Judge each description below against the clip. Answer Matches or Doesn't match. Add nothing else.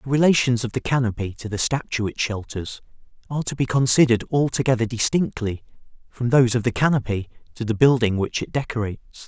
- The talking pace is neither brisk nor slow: Matches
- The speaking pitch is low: Matches